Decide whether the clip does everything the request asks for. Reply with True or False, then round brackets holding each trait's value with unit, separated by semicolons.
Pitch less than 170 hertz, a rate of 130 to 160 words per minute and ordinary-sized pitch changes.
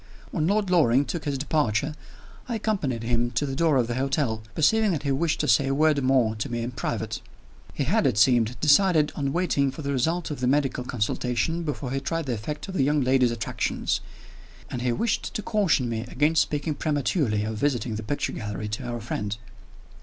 False (135 Hz; 205 wpm; 4.5 semitones)